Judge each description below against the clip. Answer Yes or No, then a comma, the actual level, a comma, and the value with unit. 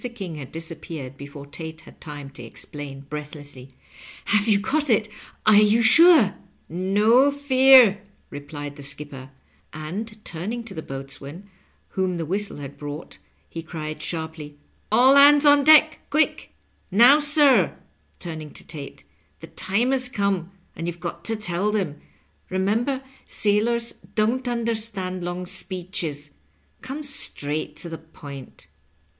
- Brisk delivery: No, average, 150 wpm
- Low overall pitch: No, medium, 185 Hz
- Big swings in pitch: Yes, wide, 7.4 semitones